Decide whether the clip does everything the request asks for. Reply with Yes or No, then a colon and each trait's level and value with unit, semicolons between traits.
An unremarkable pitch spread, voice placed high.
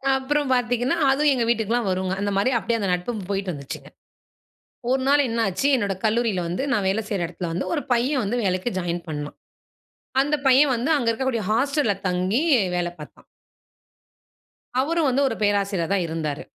No: wide, 5.9 semitones; high, 225 Hz